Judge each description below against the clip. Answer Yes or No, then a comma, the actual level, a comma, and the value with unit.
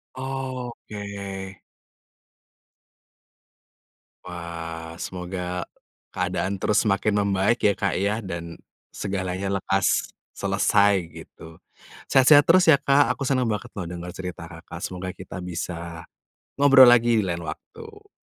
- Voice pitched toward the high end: No, very low, 95 Hz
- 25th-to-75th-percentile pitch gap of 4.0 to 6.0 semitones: Yes, average, 5.1 semitones